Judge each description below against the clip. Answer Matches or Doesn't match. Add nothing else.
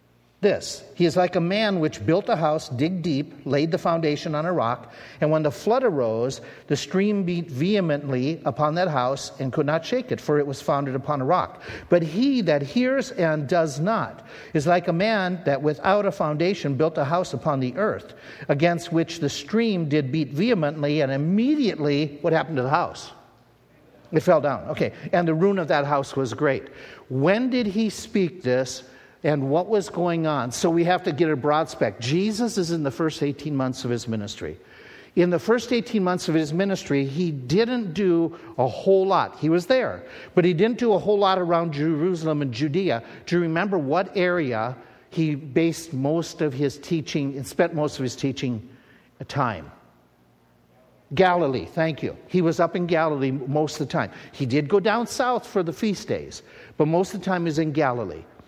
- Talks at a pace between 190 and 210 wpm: Matches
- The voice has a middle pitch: Matches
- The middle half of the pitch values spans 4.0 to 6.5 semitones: Matches